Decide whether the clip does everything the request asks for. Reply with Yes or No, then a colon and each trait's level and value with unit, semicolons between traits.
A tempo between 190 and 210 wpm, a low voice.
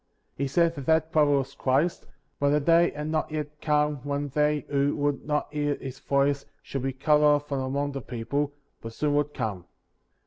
No: average, 200 wpm; medium, 145 Hz